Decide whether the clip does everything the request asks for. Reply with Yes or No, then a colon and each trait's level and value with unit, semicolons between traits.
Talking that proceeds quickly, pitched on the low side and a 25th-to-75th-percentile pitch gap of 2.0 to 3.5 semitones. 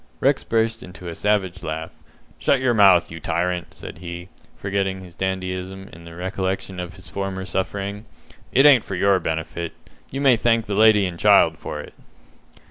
No: average, 180 wpm; very low, 95 Hz; average, 2.7 semitones